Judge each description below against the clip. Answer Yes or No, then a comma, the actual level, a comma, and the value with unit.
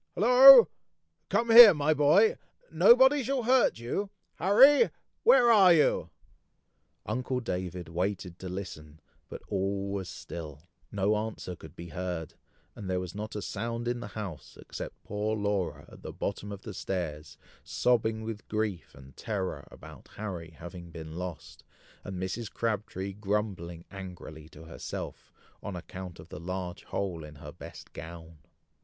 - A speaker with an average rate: Yes, average, 150 wpm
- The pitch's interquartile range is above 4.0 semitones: Yes, average, 5.0 semitones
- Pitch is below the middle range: Yes, low, 100 Hz